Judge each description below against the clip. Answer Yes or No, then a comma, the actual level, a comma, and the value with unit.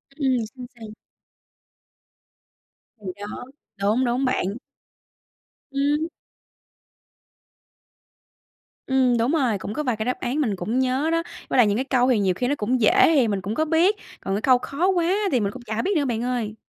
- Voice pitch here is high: Yes, very high, 250 Hz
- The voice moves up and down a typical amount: Yes, average, 4.5 semitones